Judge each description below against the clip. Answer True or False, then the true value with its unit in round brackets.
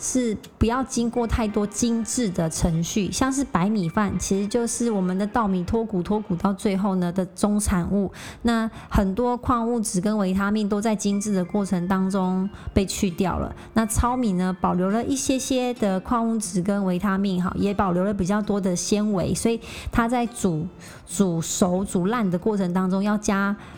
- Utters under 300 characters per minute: True (270 characters per minute)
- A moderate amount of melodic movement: True (3.2 semitones)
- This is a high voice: True (205 Hz)